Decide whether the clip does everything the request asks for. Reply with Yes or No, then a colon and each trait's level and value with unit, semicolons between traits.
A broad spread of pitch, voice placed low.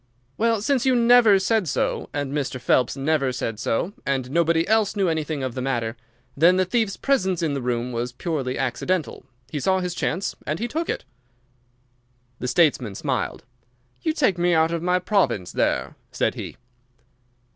No: wide, 6.9 semitones; medium, 165 Hz